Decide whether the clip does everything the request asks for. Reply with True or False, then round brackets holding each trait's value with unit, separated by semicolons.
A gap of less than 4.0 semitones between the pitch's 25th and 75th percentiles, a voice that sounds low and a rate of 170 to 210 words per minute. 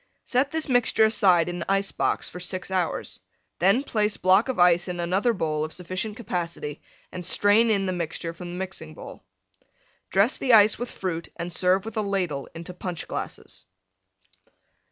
False (3.4 semitones; 185 Hz; 175 wpm)